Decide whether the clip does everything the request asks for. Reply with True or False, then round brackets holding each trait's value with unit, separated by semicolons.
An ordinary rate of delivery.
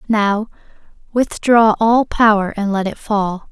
False (120 wpm)